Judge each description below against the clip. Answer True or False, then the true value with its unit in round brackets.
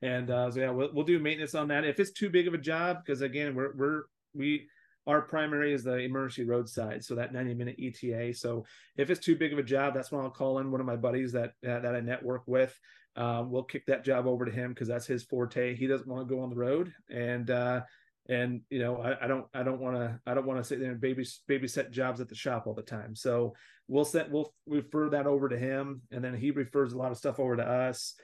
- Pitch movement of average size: False (2.3 semitones)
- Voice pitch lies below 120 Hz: False (130 Hz)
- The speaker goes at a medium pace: False (260 wpm)